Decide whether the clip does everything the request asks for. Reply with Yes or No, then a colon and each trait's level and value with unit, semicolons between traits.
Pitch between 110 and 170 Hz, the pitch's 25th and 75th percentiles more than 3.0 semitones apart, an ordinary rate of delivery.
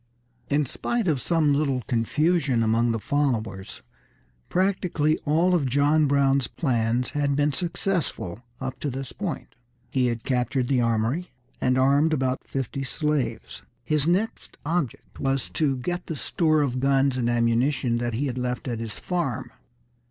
Yes: low, 135 Hz; average, 3.9 semitones; average, 150 wpm